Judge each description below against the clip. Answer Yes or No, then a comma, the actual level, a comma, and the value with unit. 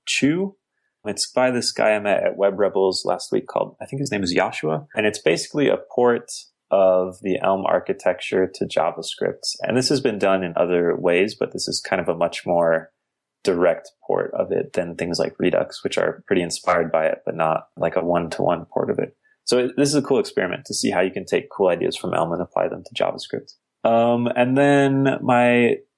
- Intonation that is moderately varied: No, wide, 5.9 semitones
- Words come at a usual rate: No, fast, 215 wpm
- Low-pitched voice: Yes, low, 110 Hz